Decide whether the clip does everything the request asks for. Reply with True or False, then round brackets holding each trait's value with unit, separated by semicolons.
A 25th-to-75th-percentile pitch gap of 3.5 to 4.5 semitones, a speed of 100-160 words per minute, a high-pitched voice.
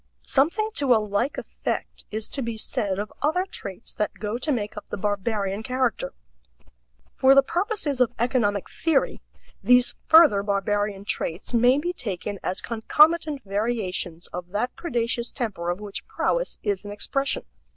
False (5.1 semitones; 155 wpm; 230 Hz)